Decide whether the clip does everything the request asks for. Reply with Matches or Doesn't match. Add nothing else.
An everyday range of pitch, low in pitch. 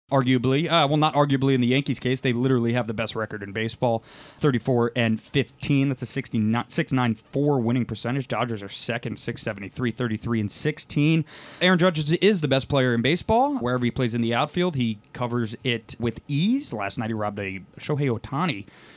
Matches